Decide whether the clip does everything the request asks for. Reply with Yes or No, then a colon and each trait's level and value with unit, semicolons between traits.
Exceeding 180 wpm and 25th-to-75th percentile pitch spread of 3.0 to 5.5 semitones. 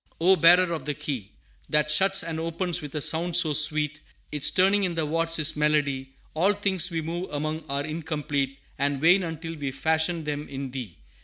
No: average, 190 wpm; narrow, 2.5 semitones